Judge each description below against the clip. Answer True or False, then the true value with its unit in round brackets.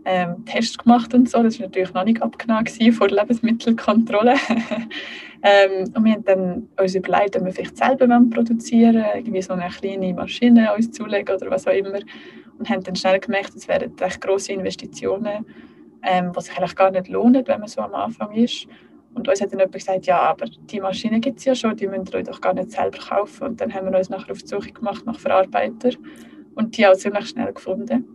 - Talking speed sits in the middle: False (215 wpm)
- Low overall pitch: False (210 Hz)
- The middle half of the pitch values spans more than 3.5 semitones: True (4.0 semitones)